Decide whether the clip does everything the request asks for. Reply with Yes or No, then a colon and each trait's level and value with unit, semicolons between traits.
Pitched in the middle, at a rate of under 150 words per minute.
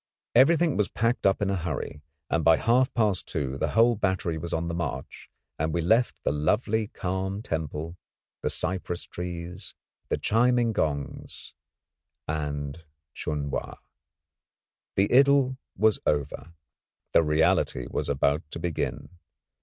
No: very low, 90 Hz; average, 140 wpm